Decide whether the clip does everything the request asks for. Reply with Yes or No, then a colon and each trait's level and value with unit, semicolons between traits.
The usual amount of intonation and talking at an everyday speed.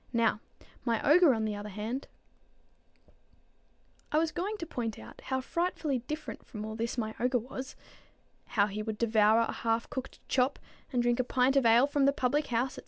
Yes: average, 3.6 semitones; average, 195 wpm